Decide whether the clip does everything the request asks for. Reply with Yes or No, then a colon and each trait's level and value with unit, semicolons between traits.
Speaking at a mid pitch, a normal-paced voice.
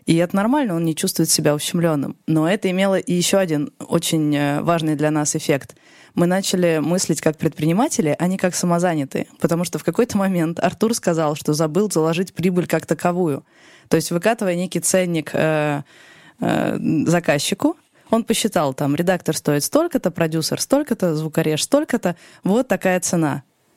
Yes: medium, 170 Hz; average, 150 wpm